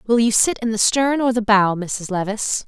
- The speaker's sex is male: No, female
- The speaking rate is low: No, fast, 245 wpm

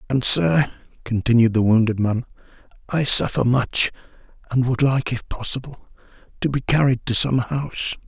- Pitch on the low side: Yes, low, 125 Hz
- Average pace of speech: Yes, average, 150 wpm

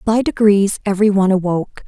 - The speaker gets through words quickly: No, average, 160 wpm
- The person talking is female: Yes, female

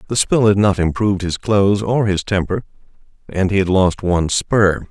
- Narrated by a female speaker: No, male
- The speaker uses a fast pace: No, average, 195 wpm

